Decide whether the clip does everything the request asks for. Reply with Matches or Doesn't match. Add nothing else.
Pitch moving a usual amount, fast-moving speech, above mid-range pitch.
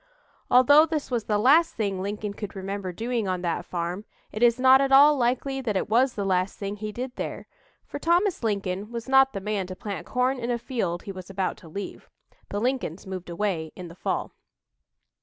Matches